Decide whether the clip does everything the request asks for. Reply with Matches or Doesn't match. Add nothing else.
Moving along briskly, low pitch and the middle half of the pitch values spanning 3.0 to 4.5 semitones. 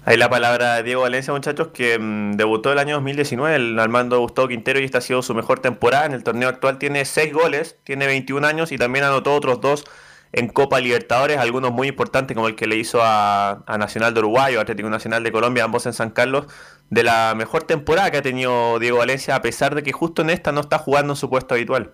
Matches